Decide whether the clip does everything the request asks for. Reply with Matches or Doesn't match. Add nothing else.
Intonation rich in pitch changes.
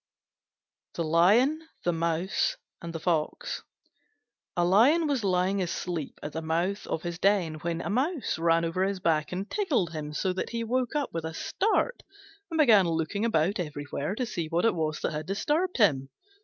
Matches